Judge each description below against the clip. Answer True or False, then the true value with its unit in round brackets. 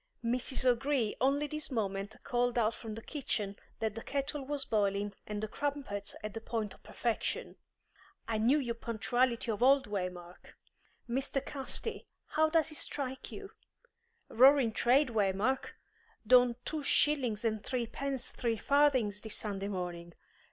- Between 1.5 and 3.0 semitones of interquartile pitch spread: False (4.5 semitones)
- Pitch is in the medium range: False (240 Hz)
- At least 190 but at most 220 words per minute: False (145 wpm)